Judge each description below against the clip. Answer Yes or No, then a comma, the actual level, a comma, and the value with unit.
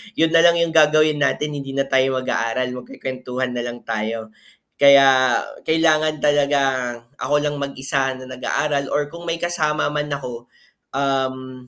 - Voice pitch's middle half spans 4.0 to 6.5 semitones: No, average, 2.8 semitones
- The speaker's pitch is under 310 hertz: Yes, medium, 140 Hz